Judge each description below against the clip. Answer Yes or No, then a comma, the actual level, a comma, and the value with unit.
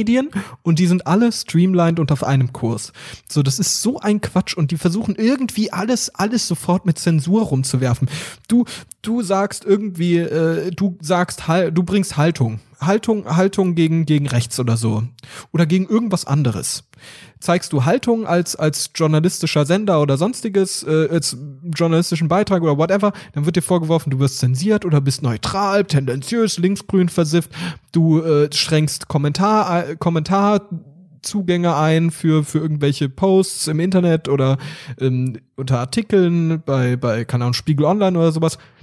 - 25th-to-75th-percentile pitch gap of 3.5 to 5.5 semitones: Yes, average, 4.6 semitones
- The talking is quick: No, average, 155 wpm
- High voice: No, medium, 165 Hz